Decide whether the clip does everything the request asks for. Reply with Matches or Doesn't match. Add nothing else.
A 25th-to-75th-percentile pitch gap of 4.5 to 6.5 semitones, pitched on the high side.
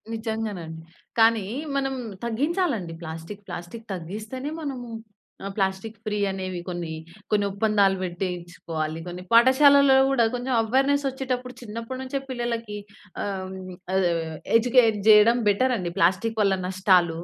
Matches